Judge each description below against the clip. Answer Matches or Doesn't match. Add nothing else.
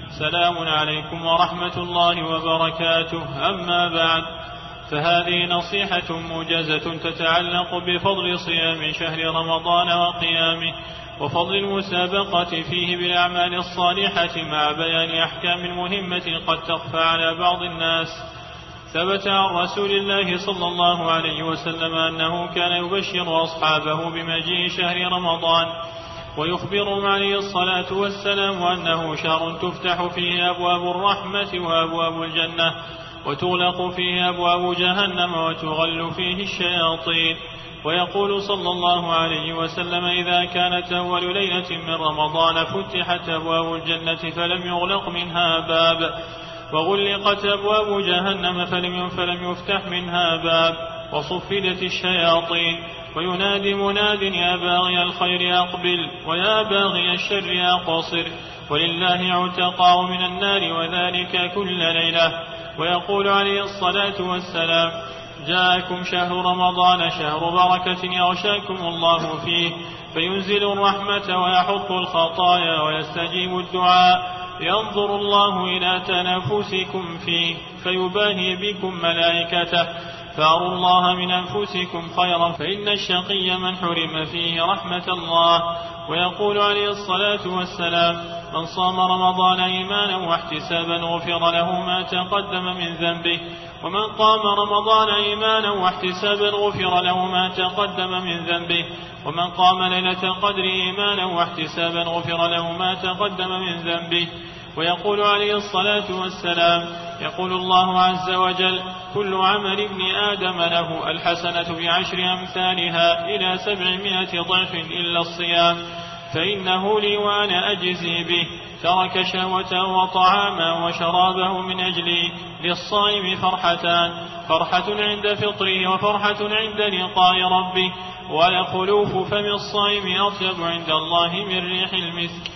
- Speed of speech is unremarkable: Matches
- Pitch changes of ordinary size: Doesn't match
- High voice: Doesn't match